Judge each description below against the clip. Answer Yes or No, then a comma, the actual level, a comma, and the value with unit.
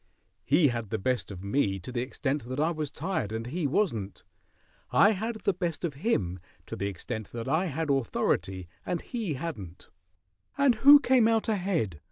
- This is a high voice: No, medium, 145 Hz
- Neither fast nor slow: Yes, average, 190 wpm